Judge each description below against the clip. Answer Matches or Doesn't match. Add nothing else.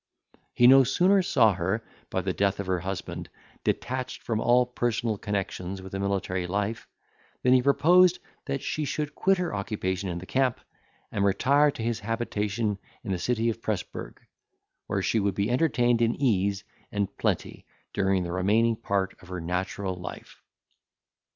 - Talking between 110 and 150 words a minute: Doesn't match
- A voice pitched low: Matches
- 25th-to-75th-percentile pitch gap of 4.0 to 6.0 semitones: Matches